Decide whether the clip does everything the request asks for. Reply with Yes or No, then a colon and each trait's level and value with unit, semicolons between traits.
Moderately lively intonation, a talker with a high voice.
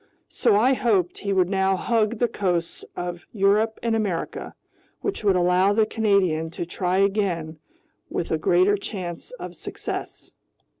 Yes: average, 3.3 semitones; high, 195 Hz